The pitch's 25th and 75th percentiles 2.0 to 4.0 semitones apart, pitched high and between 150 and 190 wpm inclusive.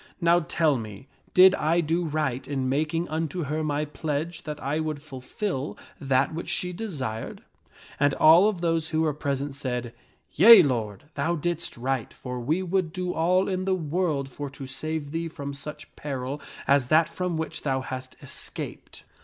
No: average, 3.6 semitones; medium, 155 Hz; average, 185 wpm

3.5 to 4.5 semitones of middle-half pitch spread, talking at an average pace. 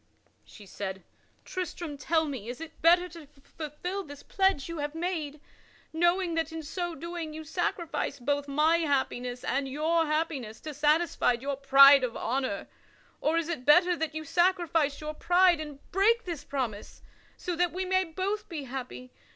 Yes: average, 3.8 semitones; average, 165 wpm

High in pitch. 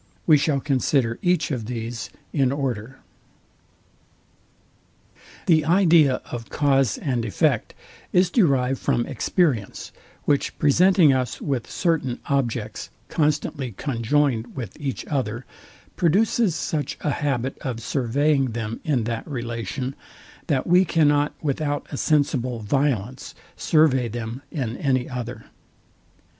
No: low, 135 Hz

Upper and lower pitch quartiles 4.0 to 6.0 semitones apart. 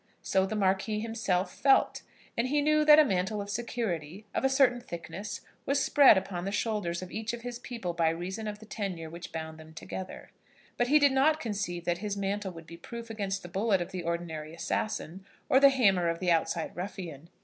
Yes: average, 5.2 semitones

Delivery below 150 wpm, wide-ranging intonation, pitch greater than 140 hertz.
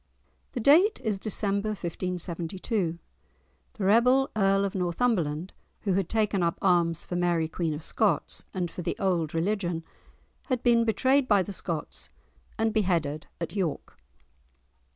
No: average, 140 wpm; average, 4.2 semitones; high, 190 Hz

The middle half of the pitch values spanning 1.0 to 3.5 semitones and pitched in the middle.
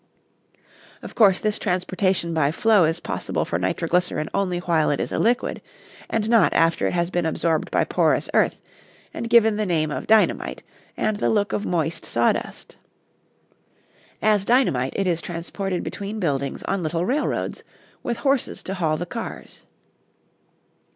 No: average, 4.5 semitones; medium, 180 Hz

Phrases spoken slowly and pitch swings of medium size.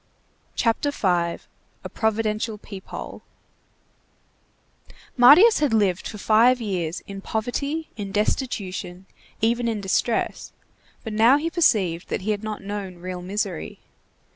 Yes: slow, 120 wpm; average, 3.4 semitones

